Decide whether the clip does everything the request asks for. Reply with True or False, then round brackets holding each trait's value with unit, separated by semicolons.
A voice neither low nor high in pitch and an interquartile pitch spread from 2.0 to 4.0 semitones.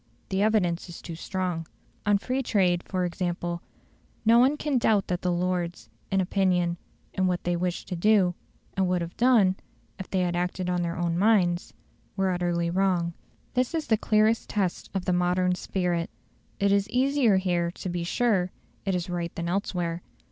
True (180 Hz; 2.4 semitones)